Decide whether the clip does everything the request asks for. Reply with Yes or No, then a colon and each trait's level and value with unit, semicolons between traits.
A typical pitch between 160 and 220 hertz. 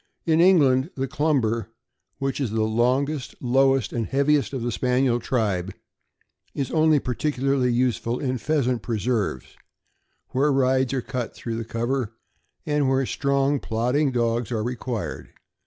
No: low, 130 Hz